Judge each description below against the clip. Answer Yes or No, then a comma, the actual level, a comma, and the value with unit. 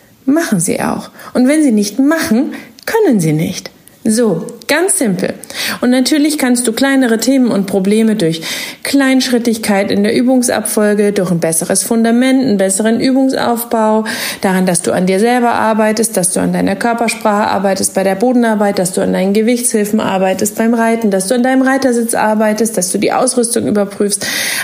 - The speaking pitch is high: Yes, high, 225 Hz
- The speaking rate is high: No, average, 170 wpm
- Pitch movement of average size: Yes, average, 3.9 semitones